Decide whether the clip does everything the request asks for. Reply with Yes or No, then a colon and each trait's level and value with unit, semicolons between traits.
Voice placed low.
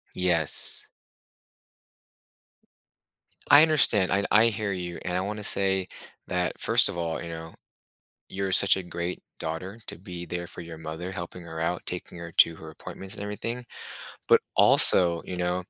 Yes: very low, 90 Hz